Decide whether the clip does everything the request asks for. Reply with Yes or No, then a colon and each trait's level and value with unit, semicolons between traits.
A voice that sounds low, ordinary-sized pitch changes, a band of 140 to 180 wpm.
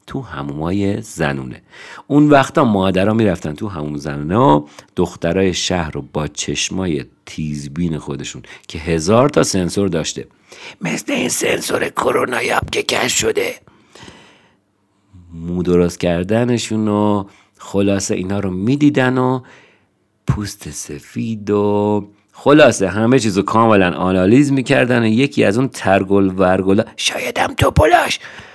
No: low, 100 Hz; average, 4.1 semitones; average, 120 wpm